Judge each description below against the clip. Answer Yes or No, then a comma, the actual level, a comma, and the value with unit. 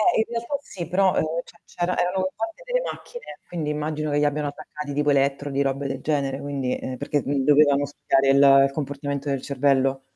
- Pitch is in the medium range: Yes, medium, 145 Hz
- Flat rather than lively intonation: No, average, 3.8 semitones